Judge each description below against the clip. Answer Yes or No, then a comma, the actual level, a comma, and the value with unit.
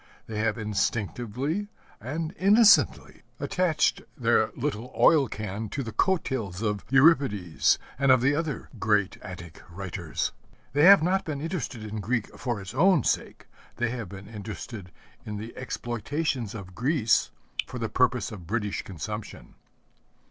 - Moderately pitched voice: No, low, 115 Hz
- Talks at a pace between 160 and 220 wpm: No, average, 140 wpm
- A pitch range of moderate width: No, wide, 5.8 semitones